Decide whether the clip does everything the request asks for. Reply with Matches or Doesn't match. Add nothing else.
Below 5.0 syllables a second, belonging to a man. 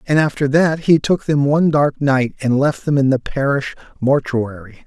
Matches